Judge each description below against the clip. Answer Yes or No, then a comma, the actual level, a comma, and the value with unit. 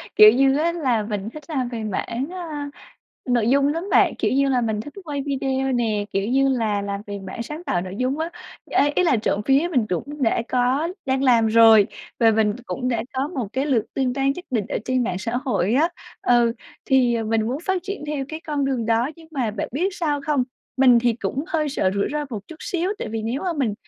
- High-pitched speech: Yes, very high, 255 Hz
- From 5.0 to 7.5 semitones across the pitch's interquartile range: No, average, 4.4 semitones